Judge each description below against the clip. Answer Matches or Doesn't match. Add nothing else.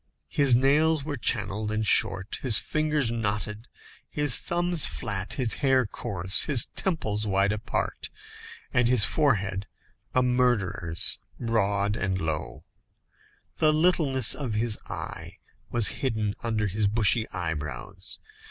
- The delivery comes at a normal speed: Doesn't match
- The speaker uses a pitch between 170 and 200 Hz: Doesn't match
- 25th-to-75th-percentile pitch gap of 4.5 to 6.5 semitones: Matches